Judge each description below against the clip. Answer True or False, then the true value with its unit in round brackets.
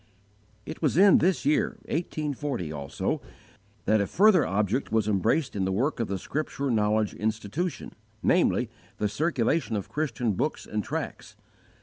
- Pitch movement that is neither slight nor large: False (6.7 semitones)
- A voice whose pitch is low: True (120 Hz)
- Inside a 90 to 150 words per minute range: True (145 wpm)